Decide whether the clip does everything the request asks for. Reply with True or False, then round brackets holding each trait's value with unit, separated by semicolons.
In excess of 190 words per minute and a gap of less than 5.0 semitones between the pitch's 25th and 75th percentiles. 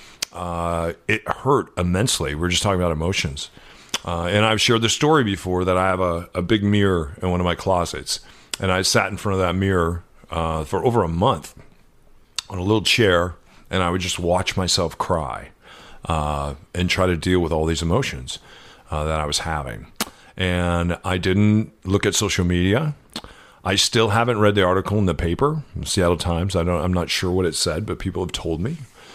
True (200 wpm; 2.7 semitones)